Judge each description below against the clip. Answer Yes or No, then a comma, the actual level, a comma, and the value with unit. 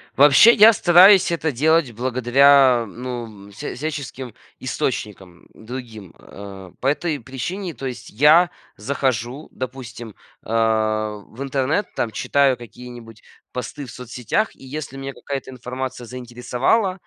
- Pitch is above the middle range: No, low, 130 Hz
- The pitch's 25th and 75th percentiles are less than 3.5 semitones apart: No, average, 3.8 semitones